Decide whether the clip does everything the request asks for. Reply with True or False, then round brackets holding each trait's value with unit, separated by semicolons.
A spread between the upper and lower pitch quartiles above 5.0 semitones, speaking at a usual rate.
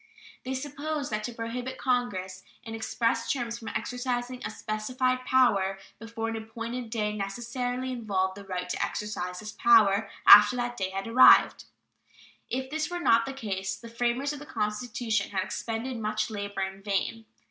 False (3.3 semitones; 165 wpm)